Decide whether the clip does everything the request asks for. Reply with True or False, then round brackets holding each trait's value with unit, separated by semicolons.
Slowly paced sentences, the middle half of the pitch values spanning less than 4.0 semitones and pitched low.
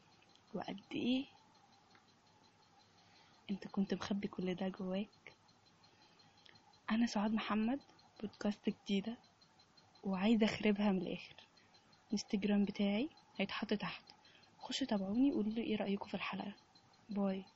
False (100 wpm; 2.4 semitones; 210 Hz)